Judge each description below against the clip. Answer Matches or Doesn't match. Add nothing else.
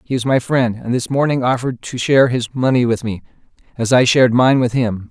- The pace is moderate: Doesn't match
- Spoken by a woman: Doesn't match